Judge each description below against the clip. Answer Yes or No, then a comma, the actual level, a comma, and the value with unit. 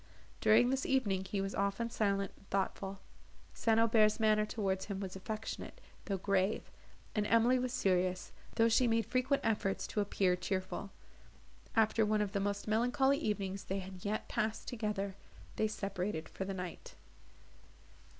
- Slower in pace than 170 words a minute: Yes, average, 155 wpm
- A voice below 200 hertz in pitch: No, high, 210 Hz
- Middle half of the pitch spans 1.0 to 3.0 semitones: Yes, narrow, 2.6 semitones